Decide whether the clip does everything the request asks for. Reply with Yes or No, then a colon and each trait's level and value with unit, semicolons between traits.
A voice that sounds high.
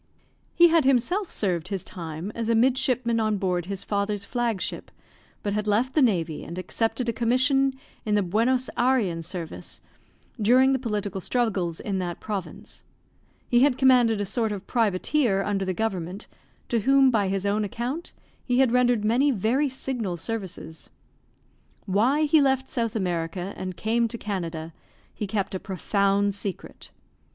Yes: high, 215 Hz